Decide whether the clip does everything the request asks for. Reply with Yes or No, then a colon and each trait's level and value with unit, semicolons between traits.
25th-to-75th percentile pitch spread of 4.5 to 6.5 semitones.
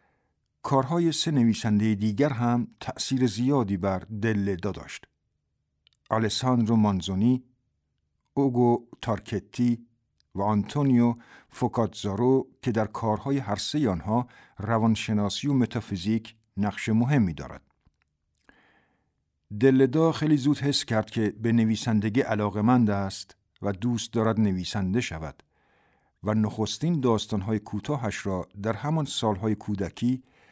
No: average, 3.5 semitones